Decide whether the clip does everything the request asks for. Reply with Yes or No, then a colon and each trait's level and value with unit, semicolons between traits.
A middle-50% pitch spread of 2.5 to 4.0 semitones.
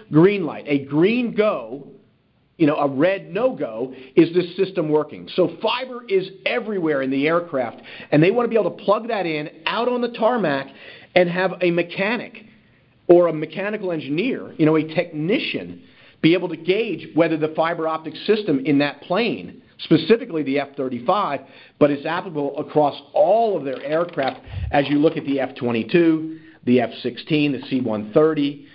No: average, 4.7 semitones